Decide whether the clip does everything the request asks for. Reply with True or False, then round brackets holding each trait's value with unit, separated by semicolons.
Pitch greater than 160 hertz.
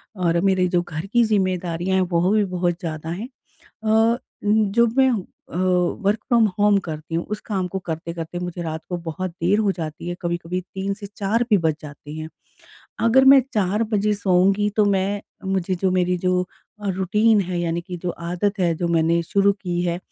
True (185 Hz)